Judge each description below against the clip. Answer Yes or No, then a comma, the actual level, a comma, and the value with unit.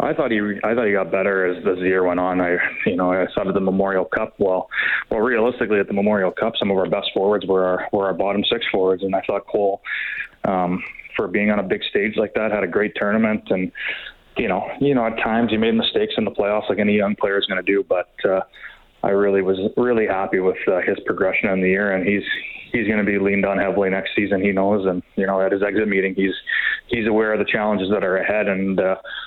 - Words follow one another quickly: Yes, fast, 250 wpm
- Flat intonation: Yes, narrow, 1.8 semitones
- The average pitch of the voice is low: Yes, low, 100 Hz